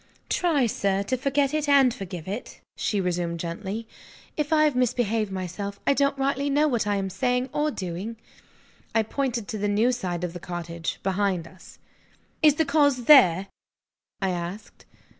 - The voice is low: No, high, 215 Hz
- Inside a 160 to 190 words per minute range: Yes, average, 170 wpm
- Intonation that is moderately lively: No, wide, 6.7 semitones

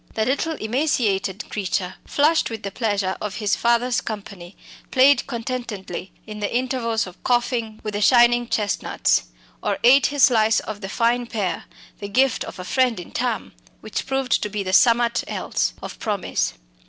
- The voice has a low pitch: No, high, 225 Hz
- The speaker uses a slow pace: No, average, 165 wpm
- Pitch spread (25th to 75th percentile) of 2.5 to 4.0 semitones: Yes, average, 3.5 semitones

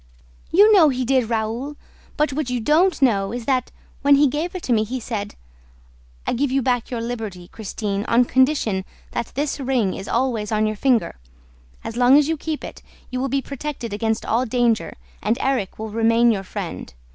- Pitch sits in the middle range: No, high, 245 Hz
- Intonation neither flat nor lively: Yes, average, 3.8 semitones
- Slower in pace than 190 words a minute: No, average, 195 wpm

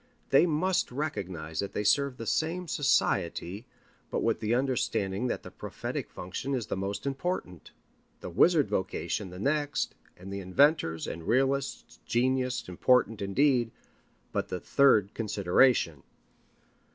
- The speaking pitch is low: Yes, low, 120 Hz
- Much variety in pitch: Yes, wide, 6.3 semitones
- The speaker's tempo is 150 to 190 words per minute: No, slow, 135 wpm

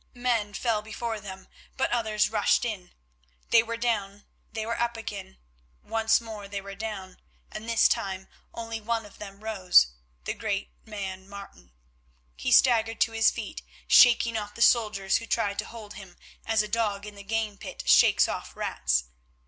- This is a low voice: No, high, 215 Hz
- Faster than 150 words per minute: Yes, average, 175 wpm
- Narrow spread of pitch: Yes, narrow, 2.3 semitones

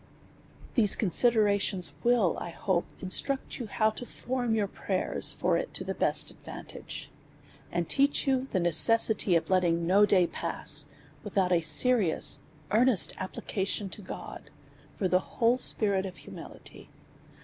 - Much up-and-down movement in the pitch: No, average, 4.2 semitones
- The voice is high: Yes, high, 200 Hz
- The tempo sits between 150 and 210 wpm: No, average, 140 wpm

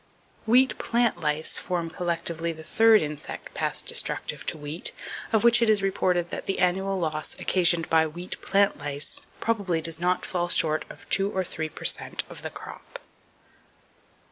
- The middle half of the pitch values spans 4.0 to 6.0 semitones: No, average, 3.5 semitones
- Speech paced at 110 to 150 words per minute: No, average, 170 wpm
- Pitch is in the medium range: Yes, medium, 175 Hz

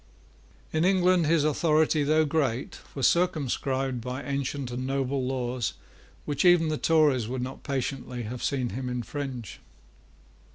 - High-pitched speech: No, low, 135 Hz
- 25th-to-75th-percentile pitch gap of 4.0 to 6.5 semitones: No, average, 3.5 semitones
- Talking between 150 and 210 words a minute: No, slow, 135 wpm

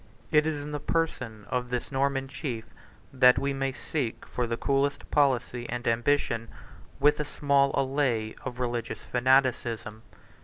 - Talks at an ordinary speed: Yes, average, 150 wpm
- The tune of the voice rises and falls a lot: No, average, 2.8 semitones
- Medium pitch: No, low, 130 Hz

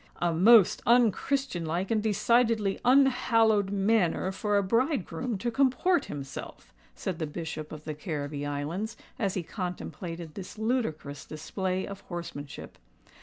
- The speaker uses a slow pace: Yes, slow, 130 wpm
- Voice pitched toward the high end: Yes, high, 195 Hz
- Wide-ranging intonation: Yes, wide, 5.8 semitones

